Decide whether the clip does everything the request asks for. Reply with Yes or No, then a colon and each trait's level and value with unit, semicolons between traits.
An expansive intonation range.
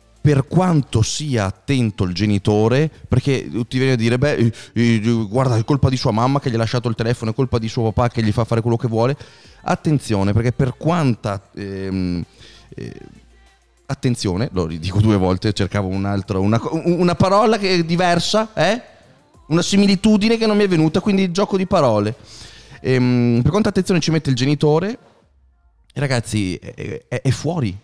Yes: wide, 6.2 semitones